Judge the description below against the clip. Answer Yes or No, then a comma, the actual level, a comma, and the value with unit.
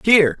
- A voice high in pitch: Yes, high, 200 Hz